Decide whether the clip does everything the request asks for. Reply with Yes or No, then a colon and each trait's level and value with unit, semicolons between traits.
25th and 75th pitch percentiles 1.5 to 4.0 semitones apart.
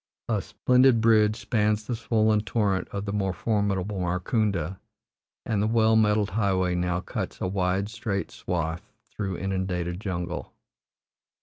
Yes: average, 3.0 semitones